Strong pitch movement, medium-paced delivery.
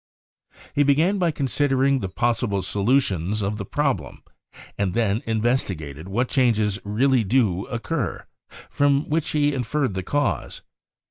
No: wide, 5.8 semitones; slow, 130 wpm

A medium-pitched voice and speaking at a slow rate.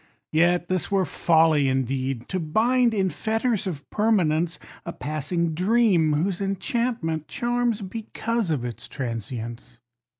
Yes: medium, 175 Hz; slow, 125 wpm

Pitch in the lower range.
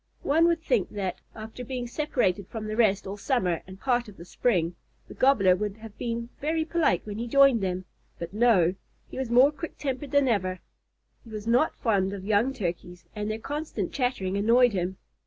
No: high, 225 Hz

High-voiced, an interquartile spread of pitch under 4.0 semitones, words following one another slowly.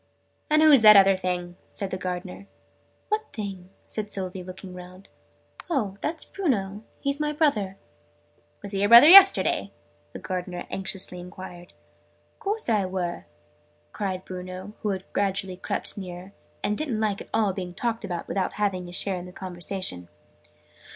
No: high, 195 Hz; average, 2.9 semitones; average, 155 wpm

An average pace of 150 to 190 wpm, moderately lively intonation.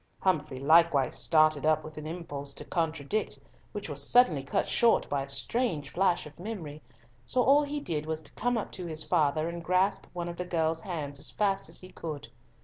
No: fast, 205 wpm; average, 3.9 semitones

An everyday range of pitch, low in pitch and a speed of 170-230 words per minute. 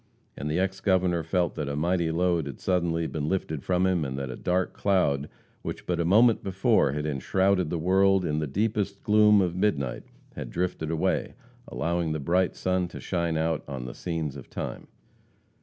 Yes: average, 3.3 semitones; very low, 85 Hz; average, 190 wpm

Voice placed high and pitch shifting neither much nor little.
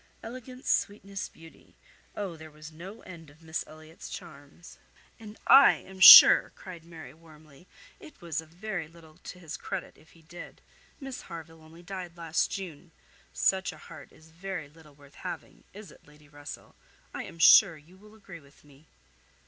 No: medium, 165 Hz; average, 3.4 semitones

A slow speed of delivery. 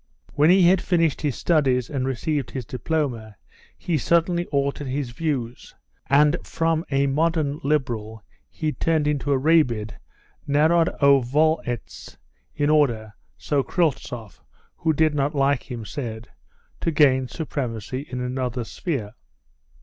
Yes: slow, 125 wpm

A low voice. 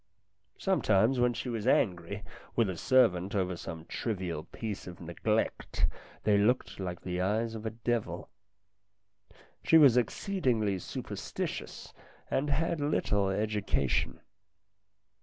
Yes: low, 105 Hz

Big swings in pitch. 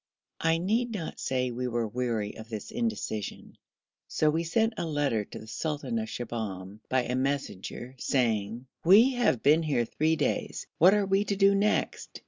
Yes: wide, 8.7 semitones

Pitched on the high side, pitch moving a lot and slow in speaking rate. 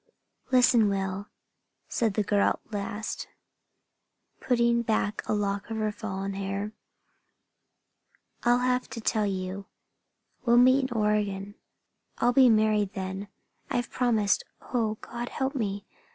No: high, 215 Hz; average, 3.2 semitones; slow, 125 wpm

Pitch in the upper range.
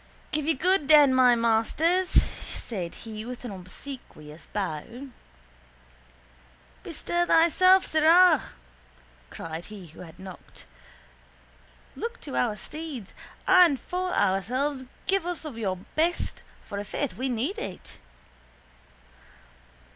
Yes: very high, 260 Hz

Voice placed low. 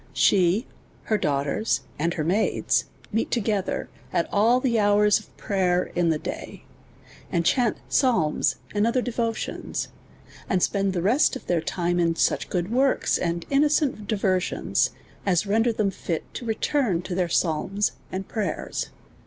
No: high, 200 Hz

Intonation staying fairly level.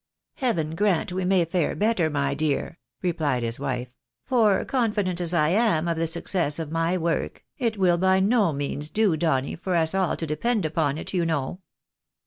No: average, 4.0 semitones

